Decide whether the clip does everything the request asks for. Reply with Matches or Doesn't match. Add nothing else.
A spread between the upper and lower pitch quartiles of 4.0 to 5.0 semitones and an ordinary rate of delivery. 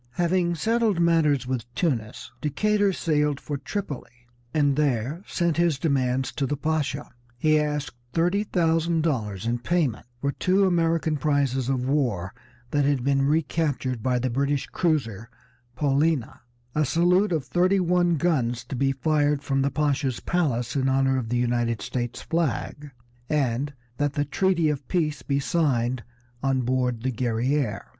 Matches